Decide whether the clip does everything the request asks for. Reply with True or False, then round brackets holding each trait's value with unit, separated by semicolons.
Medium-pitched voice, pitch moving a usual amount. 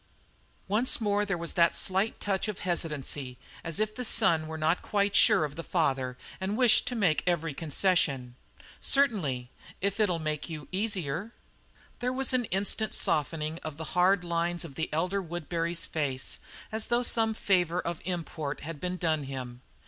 True (175 Hz; 4.6 semitones)